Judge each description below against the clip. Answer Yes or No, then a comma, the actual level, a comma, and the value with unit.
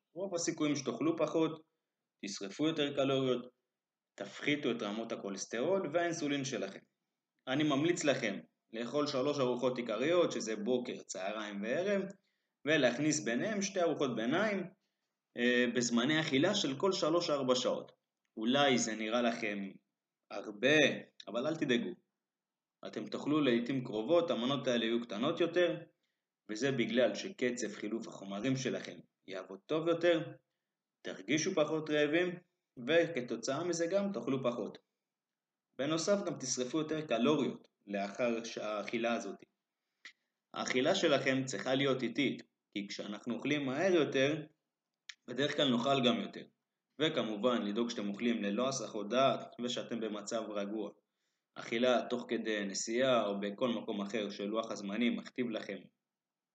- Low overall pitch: Yes, low, 125 Hz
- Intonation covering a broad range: Yes, wide, 5.7 semitones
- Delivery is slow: No, average, 120 wpm